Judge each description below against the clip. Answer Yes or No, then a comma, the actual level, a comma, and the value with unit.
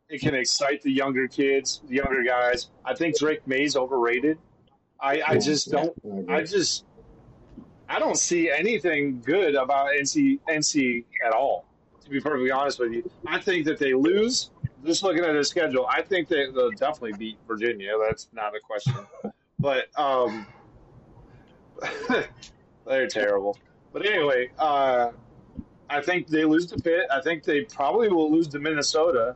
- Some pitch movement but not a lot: Yes, average, 4.2 semitones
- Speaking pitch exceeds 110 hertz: Yes, medium, 140 Hz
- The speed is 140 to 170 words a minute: Yes, average, 160 wpm